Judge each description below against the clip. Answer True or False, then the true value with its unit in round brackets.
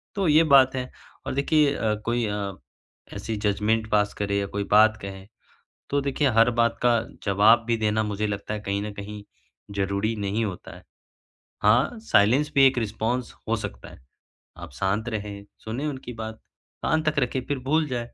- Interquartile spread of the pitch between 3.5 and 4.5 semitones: True (4.1 semitones)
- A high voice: False (110 Hz)